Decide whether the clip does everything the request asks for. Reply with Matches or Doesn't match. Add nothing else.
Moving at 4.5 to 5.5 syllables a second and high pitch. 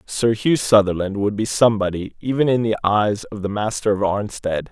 Doesn't match